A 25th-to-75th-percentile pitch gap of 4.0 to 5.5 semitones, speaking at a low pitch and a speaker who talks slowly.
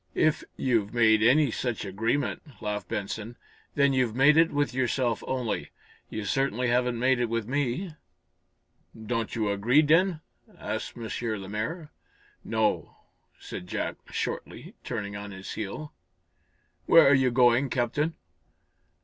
Yes: average, 4.3 semitones; low, 120 Hz; slow, 130 wpm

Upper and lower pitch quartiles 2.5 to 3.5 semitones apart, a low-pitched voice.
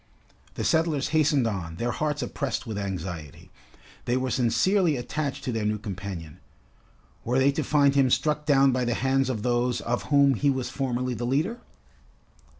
No: average, 4.1 semitones; low, 130 Hz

